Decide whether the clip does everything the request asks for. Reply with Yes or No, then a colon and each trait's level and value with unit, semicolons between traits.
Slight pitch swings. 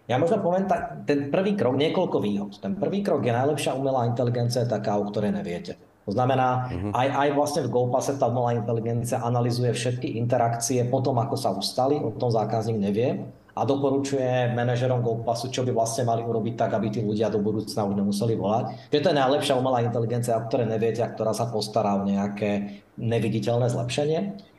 No: average, 3.0 semitones